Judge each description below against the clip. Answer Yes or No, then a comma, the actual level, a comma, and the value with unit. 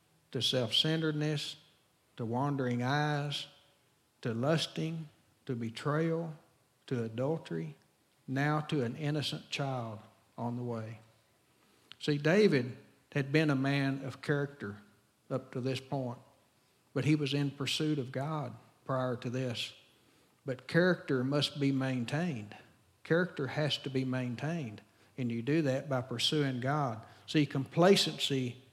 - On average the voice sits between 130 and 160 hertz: Yes, low, 135 Hz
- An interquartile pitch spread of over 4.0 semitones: No, average, 3.5 semitones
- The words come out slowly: Yes, slow, 125 wpm